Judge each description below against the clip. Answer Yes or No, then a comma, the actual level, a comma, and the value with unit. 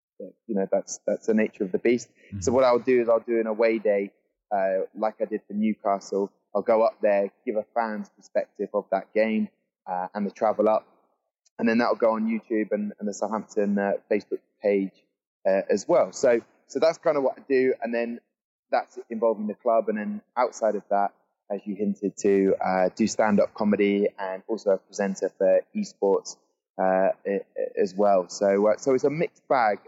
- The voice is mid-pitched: No, low, 105 Hz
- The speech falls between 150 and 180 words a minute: No, average, 200 wpm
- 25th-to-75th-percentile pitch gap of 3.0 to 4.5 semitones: No, narrow, 2.5 semitones